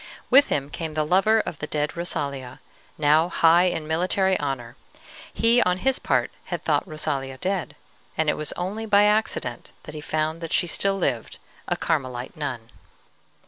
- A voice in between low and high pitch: Yes, medium, 160 Hz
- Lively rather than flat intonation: No, average, 4.5 semitones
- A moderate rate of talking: Yes, average, 170 wpm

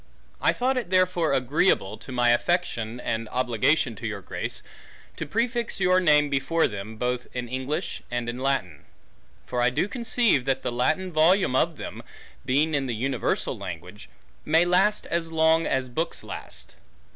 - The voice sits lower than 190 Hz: Yes, medium, 140 Hz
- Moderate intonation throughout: No, wide, 6.2 semitones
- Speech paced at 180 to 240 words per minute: No, average, 165 wpm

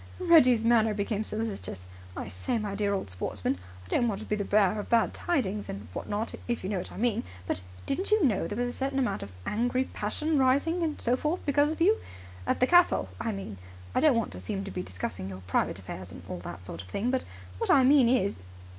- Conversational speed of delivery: No, fast, 240 wpm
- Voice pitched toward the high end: Yes, high, 220 Hz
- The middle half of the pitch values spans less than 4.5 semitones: No, wide, 5.4 semitones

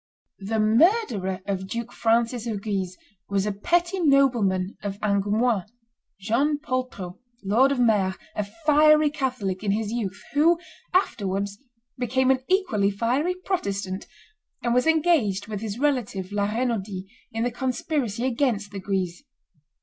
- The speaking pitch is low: No, high, 225 Hz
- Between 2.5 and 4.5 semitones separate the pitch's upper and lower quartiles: No, average, 5.1 semitones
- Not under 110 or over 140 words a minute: Yes, slow, 135 wpm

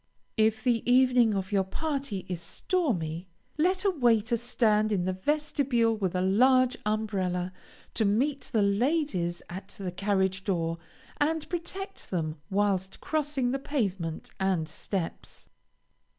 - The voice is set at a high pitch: Yes, high, 215 Hz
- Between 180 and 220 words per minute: No, slow, 135 wpm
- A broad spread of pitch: Yes, wide, 5.9 semitones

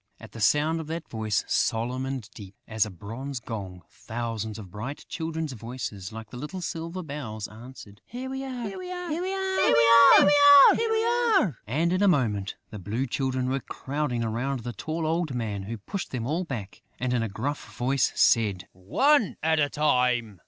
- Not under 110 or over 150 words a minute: No, average, 180 wpm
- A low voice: Yes, low, 130 Hz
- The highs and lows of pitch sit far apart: Yes, wide, 6.6 semitones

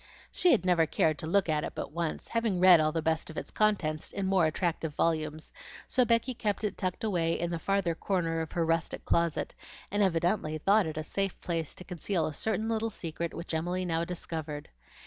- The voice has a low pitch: No, medium, 170 Hz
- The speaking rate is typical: No, fast, 210 wpm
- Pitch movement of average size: Yes, average, 3.5 semitones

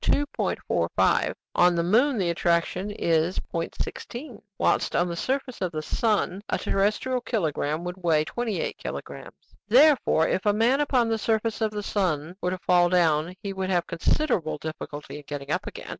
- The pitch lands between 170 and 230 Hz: Yes, medium, 185 Hz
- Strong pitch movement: No, average, 5.0 semitones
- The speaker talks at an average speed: Yes, average, 170 wpm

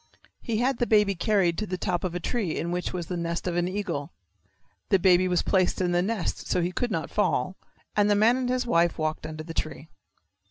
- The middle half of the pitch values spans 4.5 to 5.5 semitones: No, average, 3.5 semitones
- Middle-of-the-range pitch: Yes, medium, 180 Hz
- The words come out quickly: Yes, fast, 235 wpm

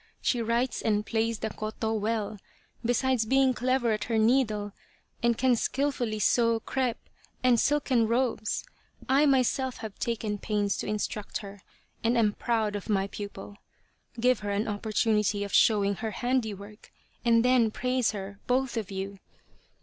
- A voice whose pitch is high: Yes, high, 225 Hz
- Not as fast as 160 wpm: Yes, average, 150 wpm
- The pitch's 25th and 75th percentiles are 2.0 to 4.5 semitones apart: Yes, average, 2.9 semitones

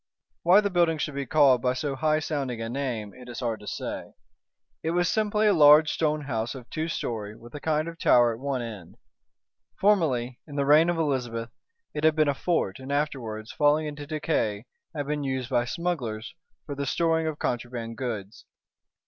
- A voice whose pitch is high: No, medium, 140 Hz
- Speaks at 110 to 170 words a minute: No, average, 195 wpm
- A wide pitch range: No, average, 4.7 semitones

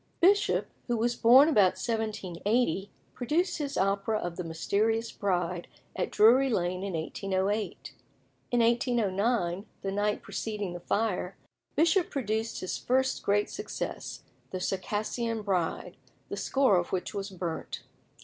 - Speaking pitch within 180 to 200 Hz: No, high, 210 Hz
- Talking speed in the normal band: No, slow, 130 wpm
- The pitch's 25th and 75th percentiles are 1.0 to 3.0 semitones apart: No, average, 4.1 semitones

